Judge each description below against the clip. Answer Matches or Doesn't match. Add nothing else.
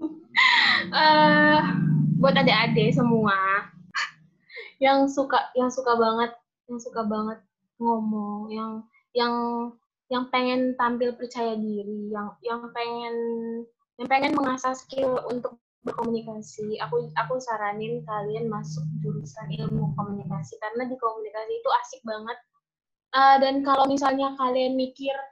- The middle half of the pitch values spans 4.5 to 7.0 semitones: Doesn't match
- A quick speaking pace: Doesn't match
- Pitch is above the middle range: Matches